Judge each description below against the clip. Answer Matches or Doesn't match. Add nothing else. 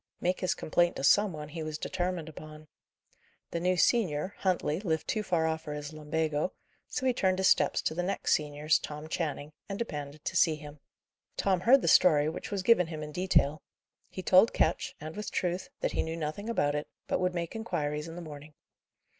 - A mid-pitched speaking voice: Matches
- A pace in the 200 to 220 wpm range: Matches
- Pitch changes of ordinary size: Matches